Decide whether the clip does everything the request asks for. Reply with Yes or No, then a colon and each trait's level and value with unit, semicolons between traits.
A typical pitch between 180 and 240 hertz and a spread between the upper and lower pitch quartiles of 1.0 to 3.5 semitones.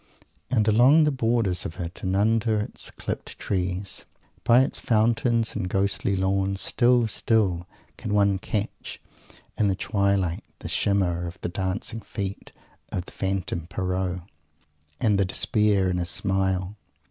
No: low, 100 Hz; average, 2.9 semitones